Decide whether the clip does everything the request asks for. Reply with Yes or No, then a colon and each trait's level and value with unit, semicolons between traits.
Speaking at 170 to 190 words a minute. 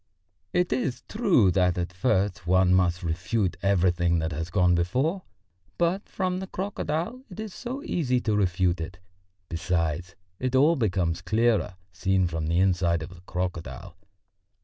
No: average, 150 wpm